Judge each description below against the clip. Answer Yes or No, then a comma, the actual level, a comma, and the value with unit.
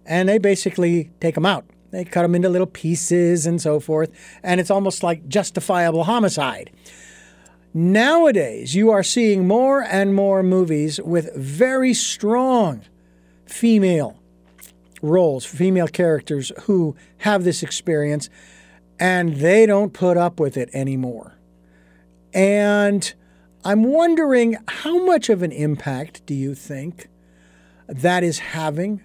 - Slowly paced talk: Yes, slow, 130 wpm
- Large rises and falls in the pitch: Yes, wide, 6.3 semitones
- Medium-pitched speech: Yes, medium, 175 Hz